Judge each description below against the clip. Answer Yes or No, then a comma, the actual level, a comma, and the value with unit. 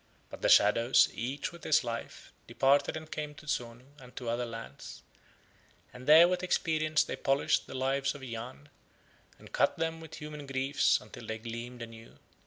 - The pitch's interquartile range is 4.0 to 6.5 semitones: Yes, average, 4.3 semitones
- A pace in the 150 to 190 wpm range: Yes, average, 175 wpm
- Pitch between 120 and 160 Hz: Yes, low, 135 Hz